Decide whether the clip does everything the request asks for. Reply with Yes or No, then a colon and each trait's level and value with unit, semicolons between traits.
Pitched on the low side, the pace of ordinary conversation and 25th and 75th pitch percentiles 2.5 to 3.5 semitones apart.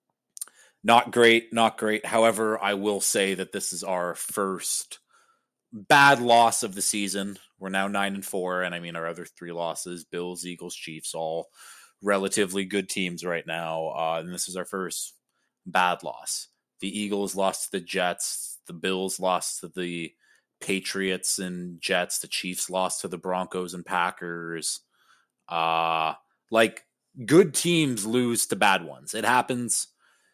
Yes: very low, 95 Hz; average, 155 wpm; average, 2.9 semitones